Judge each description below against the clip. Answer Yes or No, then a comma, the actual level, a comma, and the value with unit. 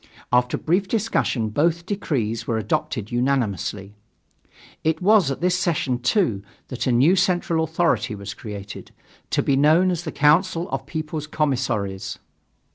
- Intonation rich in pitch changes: Yes, wide, 6.7 semitones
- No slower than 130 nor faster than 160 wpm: Yes, average, 140 wpm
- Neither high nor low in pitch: Yes, medium, 145 Hz